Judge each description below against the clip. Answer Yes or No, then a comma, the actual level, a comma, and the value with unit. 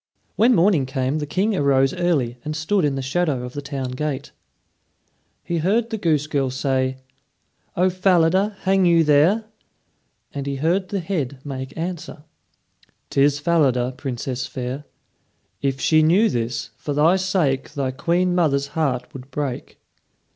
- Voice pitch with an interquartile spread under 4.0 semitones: No, average, 4.9 semitones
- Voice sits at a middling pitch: Yes, medium, 150 Hz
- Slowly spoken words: No, average, 150 wpm